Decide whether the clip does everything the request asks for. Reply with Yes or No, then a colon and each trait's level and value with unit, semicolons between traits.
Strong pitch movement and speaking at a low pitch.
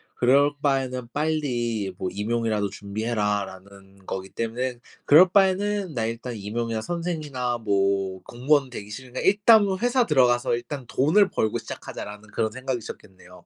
Yes: wide, 5.9 semitones; low, 120 Hz